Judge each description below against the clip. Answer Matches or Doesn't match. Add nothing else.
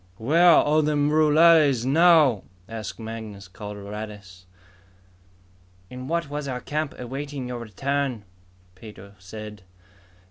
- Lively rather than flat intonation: Matches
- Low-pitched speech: Matches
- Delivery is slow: Matches